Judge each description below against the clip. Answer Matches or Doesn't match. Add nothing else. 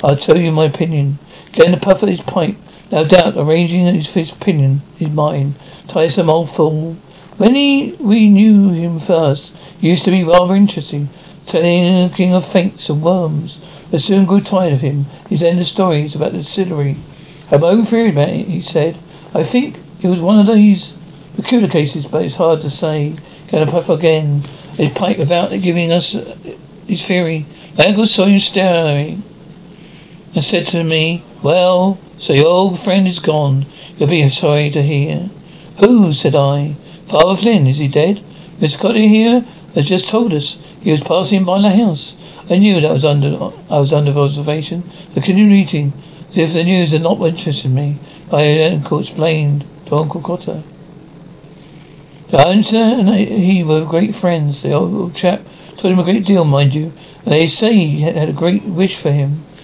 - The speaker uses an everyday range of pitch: Matches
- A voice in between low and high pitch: Matches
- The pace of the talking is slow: Doesn't match